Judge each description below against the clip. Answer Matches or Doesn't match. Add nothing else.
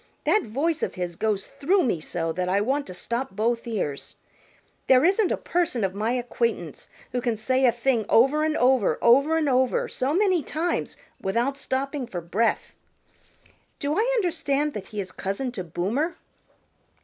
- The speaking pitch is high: Matches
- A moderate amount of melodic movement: Doesn't match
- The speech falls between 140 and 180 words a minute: Matches